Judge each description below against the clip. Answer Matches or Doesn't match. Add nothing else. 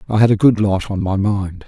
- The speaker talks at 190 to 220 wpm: Doesn't match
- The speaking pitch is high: Doesn't match